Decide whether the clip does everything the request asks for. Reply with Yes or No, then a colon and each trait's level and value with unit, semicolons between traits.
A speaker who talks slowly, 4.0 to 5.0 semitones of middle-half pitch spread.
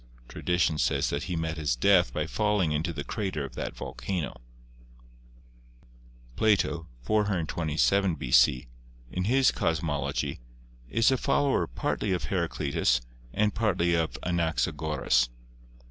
Yes: slow, 115 wpm; average, 4.6 semitones